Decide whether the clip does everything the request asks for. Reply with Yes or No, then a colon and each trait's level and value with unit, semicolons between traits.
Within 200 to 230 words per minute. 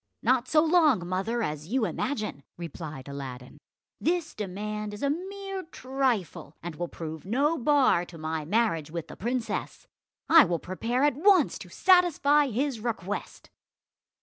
No: average, 150 wpm